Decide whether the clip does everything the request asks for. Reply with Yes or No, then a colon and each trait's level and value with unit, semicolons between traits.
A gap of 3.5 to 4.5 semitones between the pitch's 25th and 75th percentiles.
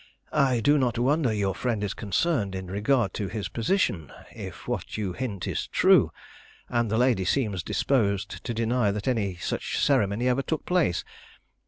Yes: average, 4.2 semitones